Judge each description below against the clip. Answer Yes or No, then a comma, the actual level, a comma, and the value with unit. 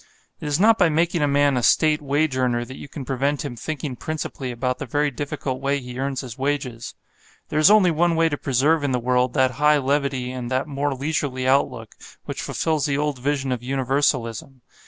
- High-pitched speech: No, medium, 140 Hz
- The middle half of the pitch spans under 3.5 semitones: Yes, narrow, 2.5 semitones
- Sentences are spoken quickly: Yes, fast, 210 wpm